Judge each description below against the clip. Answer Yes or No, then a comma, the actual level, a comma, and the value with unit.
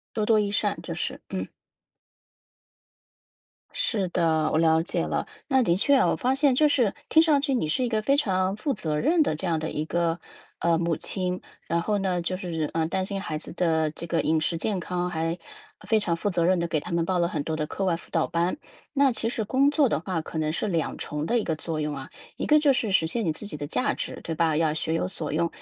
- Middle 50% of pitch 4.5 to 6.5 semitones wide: Yes, average, 5.1 semitones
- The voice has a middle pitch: Yes, medium, 175 Hz